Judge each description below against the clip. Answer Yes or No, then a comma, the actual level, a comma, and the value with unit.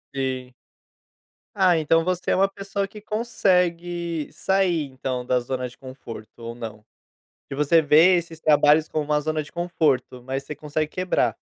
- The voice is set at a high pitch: No, medium, 155 Hz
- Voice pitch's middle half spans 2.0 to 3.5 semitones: No, average, 4.9 semitones